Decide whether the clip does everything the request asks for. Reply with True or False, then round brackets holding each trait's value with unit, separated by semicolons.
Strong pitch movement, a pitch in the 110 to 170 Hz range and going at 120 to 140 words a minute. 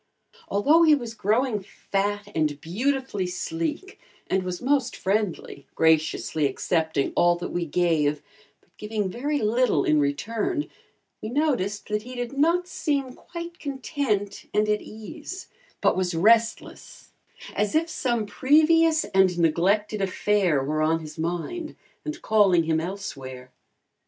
False (7.6 semitones; 210 Hz; 135 wpm)